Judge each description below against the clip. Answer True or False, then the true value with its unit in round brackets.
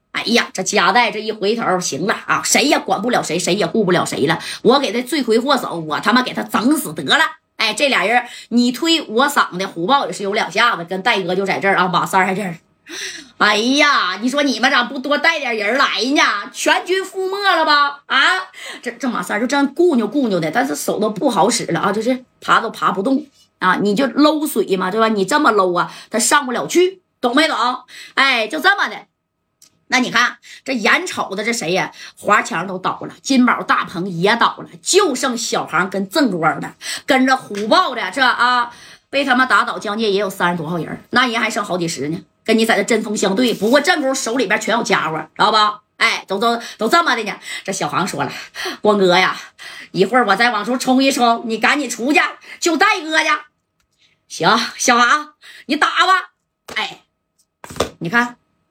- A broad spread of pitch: True (5.8 semitones)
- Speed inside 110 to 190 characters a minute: False (280 characters per minute)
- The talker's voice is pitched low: False (240 Hz)